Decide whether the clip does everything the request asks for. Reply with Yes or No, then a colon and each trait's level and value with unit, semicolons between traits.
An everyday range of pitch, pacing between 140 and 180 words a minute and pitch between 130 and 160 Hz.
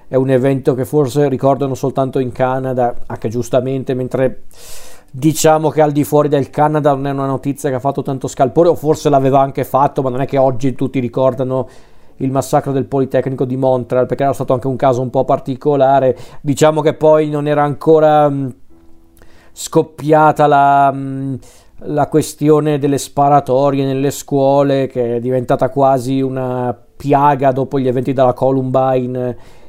No: narrow, 1.7 semitones; average, 160 wpm; low, 135 Hz